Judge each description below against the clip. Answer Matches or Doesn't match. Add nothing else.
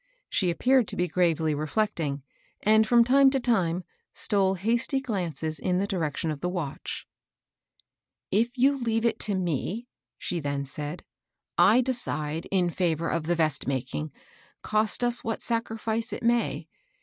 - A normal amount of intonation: Doesn't match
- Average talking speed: Matches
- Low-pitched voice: Doesn't match